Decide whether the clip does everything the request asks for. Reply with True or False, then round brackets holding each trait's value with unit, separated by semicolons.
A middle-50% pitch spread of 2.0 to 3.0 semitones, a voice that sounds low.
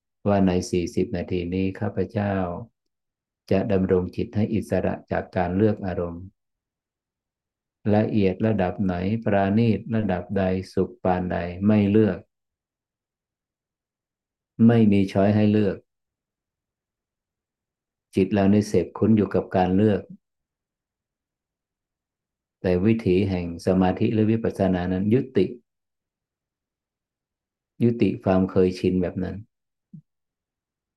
True (2.5 semitones; 95 Hz)